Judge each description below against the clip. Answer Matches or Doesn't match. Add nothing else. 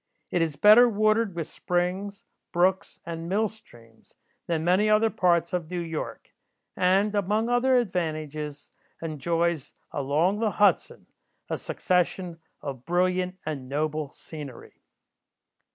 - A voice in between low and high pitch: Matches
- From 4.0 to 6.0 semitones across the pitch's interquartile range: Matches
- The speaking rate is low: Matches